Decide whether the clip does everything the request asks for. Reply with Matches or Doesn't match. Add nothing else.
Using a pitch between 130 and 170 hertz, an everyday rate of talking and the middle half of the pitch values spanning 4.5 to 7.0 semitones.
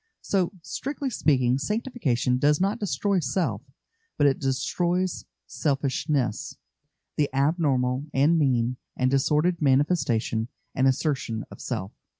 Doesn't match